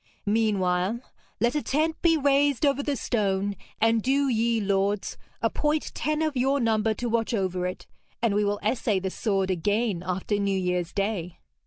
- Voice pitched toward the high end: Yes, high, 215 Hz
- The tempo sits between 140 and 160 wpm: No, average, 170 wpm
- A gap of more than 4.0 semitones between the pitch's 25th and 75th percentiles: Yes, average, 5.2 semitones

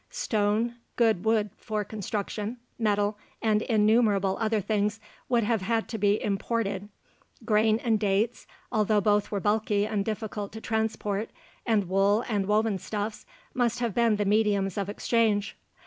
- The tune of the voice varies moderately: No, narrow, 1.5 semitones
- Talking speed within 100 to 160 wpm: Yes, average, 150 wpm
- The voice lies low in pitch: No, high, 210 Hz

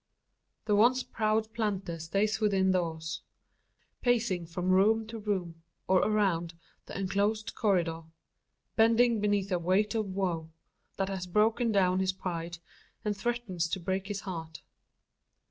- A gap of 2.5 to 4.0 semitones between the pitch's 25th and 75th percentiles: Yes, average, 3.4 semitones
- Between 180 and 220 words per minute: No, slow, 135 wpm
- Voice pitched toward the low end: No, high, 195 Hz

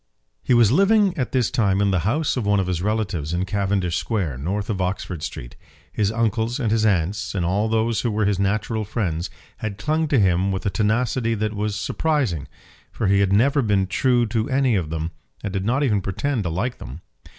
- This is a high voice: No, low, 105 Hz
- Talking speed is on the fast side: Yes, fast, 215 wpm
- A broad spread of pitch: No, average, 3.7 semitones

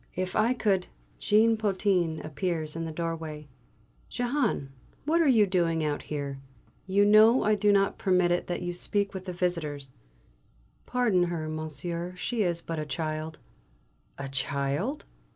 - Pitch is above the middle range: No, medium, 175 Hz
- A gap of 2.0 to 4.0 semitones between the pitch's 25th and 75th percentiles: No, average, 4.7 semitones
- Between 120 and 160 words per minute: Yes, average, 155 wpm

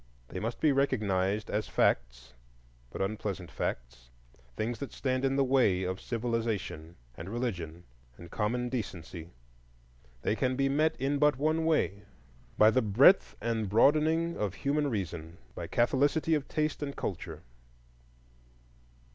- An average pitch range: No, wide, 6.8 semitones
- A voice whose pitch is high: No, low, 115 Hz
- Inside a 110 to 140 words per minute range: Yes, slow, 135 wpm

